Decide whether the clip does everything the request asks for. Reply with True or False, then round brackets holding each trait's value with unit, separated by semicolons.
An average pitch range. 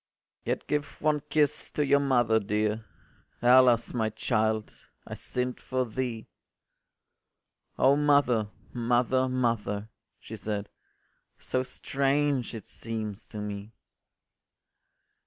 True (3.2 semitones)